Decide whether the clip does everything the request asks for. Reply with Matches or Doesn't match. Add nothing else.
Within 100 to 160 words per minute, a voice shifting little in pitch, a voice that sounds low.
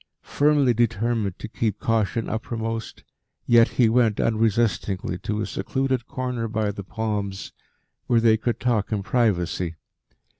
Matches